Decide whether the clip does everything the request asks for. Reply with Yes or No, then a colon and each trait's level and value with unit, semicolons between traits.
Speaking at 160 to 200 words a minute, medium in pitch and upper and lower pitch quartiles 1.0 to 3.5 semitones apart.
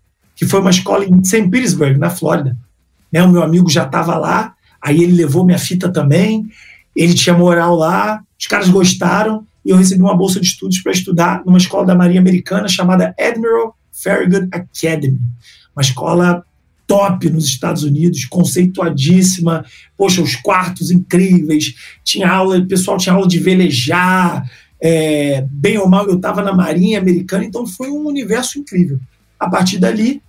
Yes: average, 165 wpm; medium, 180 Hz; average, 2.8 semitones